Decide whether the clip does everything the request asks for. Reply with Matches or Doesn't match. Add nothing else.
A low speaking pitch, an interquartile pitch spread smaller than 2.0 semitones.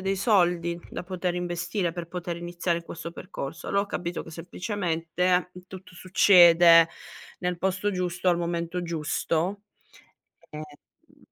Doesn't match